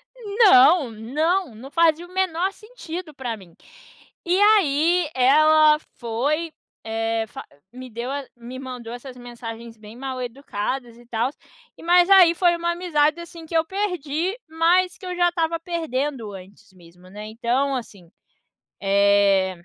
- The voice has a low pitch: No, very high, 280 Hz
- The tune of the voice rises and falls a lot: Yes, wide, 6.7 semitones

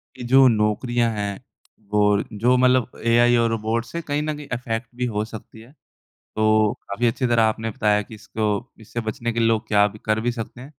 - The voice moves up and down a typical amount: No, narrow, 2.1 semitones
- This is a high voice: No, low, 115 Hz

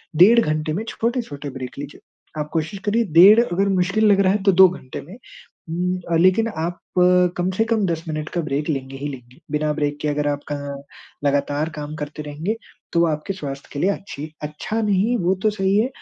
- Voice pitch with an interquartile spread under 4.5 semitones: No, average, 5.0 semitones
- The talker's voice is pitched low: No, medium, 165 Hz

